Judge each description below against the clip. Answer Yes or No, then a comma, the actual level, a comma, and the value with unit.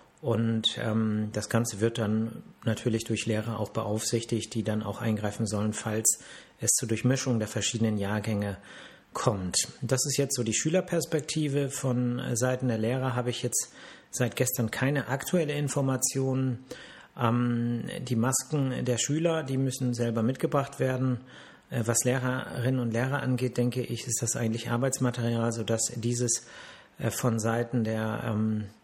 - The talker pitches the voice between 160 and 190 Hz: No, low, 120 Hz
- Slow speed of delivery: No, average, 150 wpm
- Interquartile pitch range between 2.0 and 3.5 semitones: Yes, narrow, 2.6 semitones